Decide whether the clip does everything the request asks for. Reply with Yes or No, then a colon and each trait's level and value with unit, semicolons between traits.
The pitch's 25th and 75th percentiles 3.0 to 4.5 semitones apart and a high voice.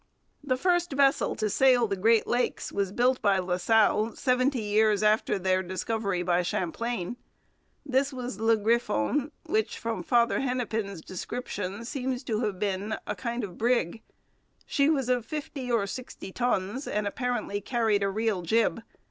Yes: average, 3.9 semitones; high, 225 Hz